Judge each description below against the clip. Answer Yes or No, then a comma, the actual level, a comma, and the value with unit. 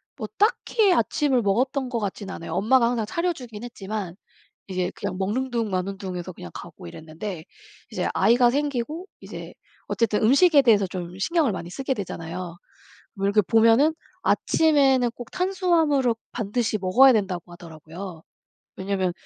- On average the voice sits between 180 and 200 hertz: No, high, 220 Hz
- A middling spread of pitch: No, wide, 6.0 semitones